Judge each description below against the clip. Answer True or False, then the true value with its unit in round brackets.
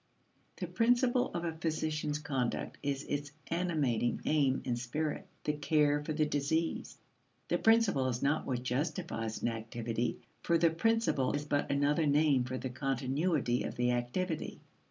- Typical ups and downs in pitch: True (3.9 semitones)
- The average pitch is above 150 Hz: False (145 Hz)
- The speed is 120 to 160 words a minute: True (155 wpm)